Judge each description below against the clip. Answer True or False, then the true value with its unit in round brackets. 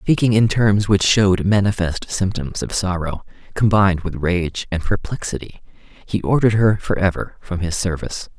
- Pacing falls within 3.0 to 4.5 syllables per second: False (4.9 syllables/s)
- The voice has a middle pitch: False (95 Hz)